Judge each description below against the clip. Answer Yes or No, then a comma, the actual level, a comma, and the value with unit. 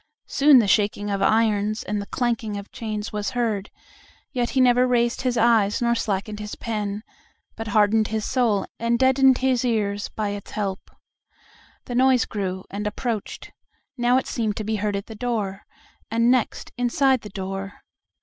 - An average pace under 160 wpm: No, average, 170 wpm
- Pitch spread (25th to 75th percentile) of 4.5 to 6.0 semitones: No, average, 2.9 semitones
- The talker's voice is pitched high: Yes, high, 220 Hz